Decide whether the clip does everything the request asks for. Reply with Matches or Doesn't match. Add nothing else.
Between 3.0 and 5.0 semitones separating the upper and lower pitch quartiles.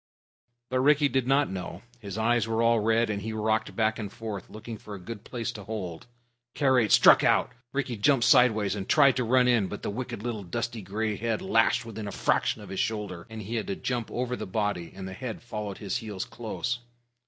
Doesn't match